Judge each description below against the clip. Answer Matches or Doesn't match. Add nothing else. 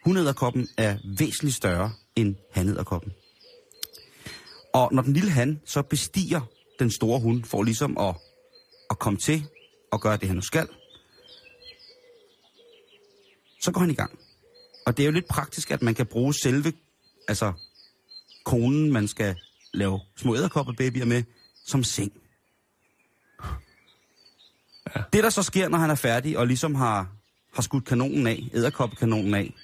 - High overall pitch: Doesn't match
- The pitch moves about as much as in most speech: Doesn't match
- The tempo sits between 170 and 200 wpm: Doesn't match